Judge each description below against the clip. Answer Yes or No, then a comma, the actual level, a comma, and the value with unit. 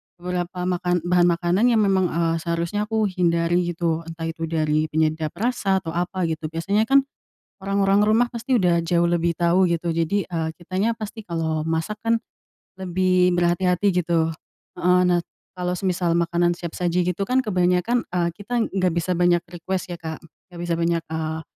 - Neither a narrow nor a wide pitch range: No, narrow, 2.0 semitones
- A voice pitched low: No, medium, 175 Hz